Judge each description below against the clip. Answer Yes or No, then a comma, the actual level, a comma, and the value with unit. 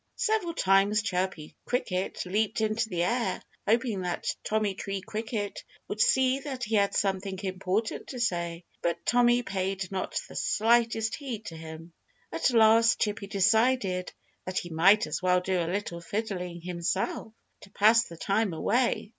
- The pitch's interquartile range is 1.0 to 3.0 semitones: No, average, 3.8 semitones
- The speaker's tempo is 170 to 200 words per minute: No, average, 155 wpm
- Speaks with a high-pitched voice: Yes, high, 200 Hz